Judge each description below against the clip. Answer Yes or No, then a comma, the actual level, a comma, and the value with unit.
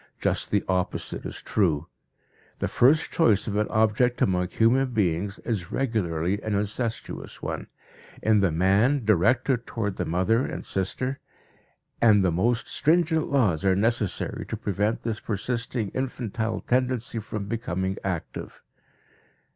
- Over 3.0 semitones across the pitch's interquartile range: Yes, average, 4.1 semitones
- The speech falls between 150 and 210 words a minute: No, slow, 135 wpm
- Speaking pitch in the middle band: No, low, 110 Hz